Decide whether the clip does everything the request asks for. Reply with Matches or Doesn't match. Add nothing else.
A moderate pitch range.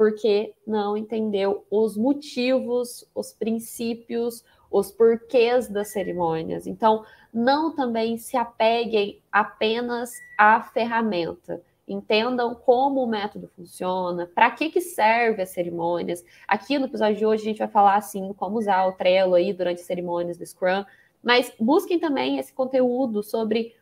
Matches